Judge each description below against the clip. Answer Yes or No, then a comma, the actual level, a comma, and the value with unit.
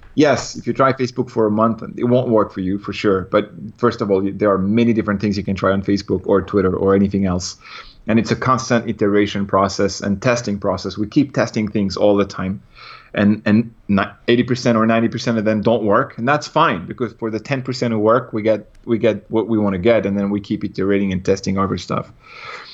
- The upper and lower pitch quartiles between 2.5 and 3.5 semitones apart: Yes, average, 2.9 semitones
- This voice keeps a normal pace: No, fast, 225 wpm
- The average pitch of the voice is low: Yes, low, 105 Hz